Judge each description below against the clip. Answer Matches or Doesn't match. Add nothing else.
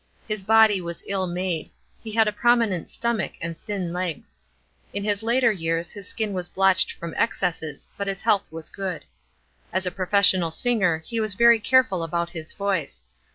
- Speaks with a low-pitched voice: Doesn't match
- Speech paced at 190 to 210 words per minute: Doesn't match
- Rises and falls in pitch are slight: Doesn't match